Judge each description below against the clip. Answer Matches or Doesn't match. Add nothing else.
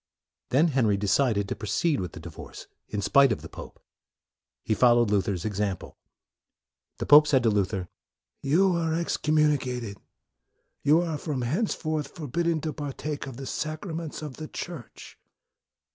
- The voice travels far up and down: Matches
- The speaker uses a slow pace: Doesn't match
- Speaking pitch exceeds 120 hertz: Matches